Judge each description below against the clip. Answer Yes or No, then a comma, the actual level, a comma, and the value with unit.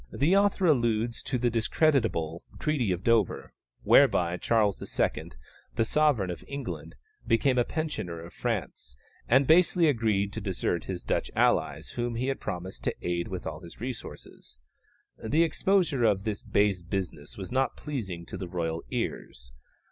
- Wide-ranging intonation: Yes, wide, 7.1 semitones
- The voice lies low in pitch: Yes, low, 110 Hz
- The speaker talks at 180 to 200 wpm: No, average, 155 wpm